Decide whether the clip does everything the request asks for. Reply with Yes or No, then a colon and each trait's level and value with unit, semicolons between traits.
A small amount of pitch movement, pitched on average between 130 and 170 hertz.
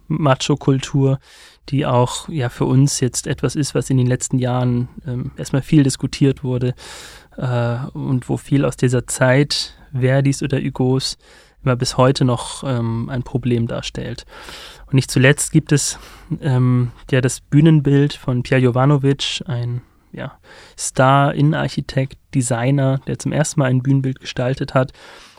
Yes: narrow, 2.0 semitones; low, 135 Hz